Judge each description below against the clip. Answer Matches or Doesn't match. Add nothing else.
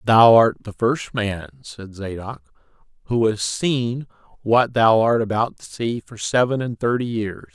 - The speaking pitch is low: Matches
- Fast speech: Doesn't match